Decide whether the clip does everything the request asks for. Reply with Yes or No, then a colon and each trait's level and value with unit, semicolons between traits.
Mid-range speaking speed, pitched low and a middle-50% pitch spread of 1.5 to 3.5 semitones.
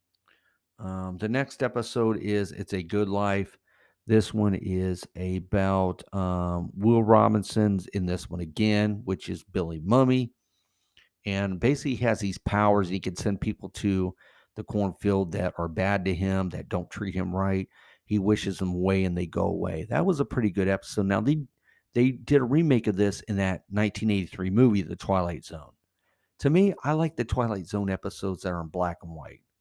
Yes: average, 180 wpm; low, 100 Hz; average, 2.8 semitones